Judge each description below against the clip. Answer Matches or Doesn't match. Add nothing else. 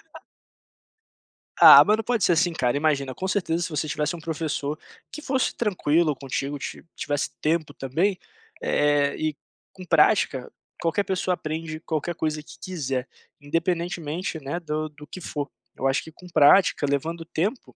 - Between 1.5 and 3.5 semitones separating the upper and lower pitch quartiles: Matches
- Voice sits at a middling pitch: Matches